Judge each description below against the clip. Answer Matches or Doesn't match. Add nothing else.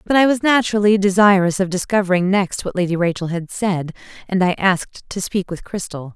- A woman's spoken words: Matches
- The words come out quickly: Doesn't match